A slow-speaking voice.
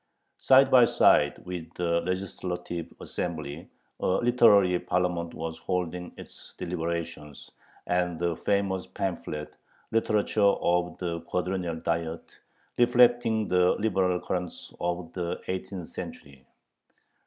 Yes: slow, 105 wpm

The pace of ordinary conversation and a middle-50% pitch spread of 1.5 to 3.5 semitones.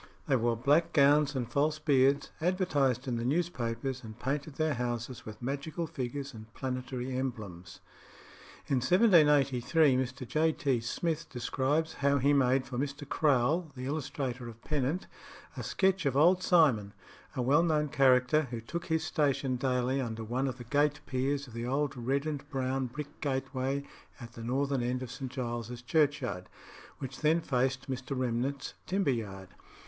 Yes: average, 165 wpm; average, 3.1 semitones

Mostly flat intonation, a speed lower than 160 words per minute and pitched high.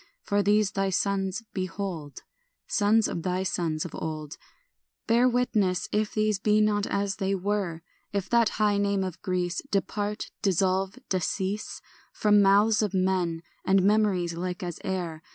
Yes: narrow, 2.3 semitones; average, 150 wpm; high, 195 Hz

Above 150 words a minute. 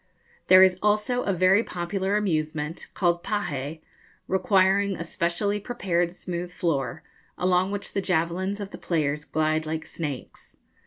No: average, 140 wpm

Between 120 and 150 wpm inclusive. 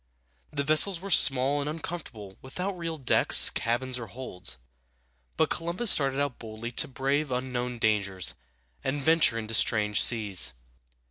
Yes: average, 140 wpm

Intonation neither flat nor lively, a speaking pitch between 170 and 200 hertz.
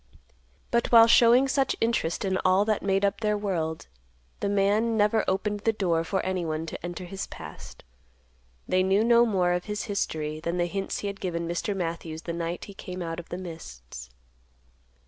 Yes: average, 3.6 semitones; high, 190 Hz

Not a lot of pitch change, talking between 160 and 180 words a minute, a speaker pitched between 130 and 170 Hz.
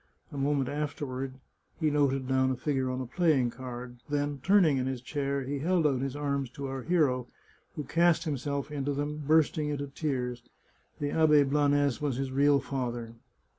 Yes: narrow, 2.2 semitones; average, 175 wpm; medium, 140 Hz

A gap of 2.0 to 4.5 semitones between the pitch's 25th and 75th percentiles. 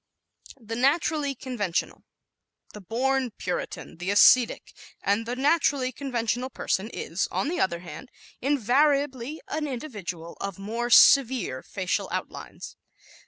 No: average, 5.3 semitones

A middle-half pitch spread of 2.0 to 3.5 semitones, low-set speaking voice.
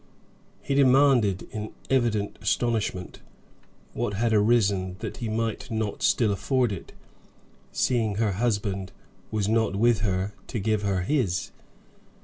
Yes: average, 3.0 semitones; low, 110 Hz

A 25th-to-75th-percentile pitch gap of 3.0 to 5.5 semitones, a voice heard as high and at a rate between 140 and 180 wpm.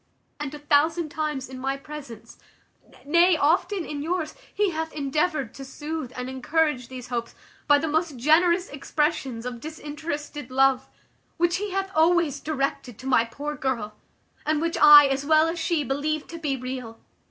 Yes: average, 3.3 semitones; very high, 295 Hz; average, 165 wpm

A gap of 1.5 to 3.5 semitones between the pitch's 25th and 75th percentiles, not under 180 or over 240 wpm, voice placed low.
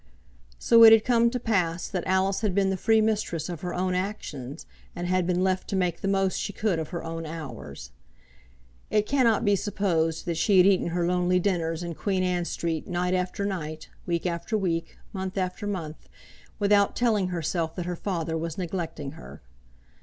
No: average, 3.1 semitones; average, 190 wpm; medium, 180 Hz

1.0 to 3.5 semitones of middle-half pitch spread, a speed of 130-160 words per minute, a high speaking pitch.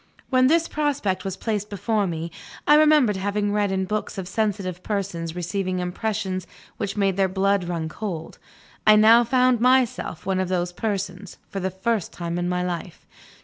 No: average, 3.2 semitones; average, 175 wpm; high, 195 Hz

